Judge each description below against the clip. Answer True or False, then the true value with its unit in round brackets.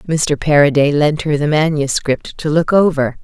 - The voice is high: False (150 Hz)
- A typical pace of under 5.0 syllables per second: True (4.6 syllables/s)